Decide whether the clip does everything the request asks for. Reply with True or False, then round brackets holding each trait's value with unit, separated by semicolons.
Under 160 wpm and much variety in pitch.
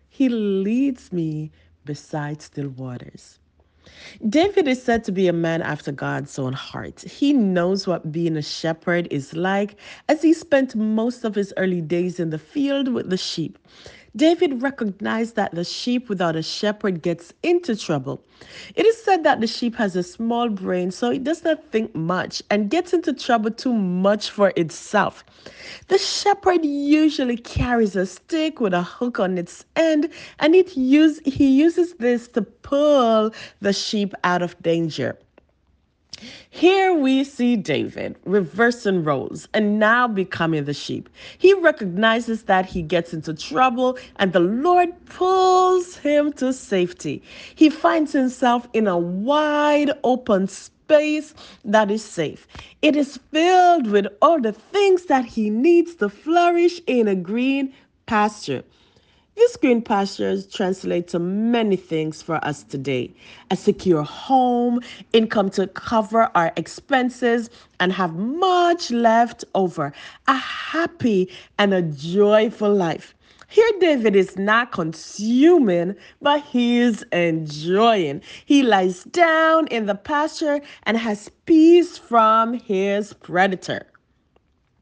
True (140 wpm; 7.9 semitones)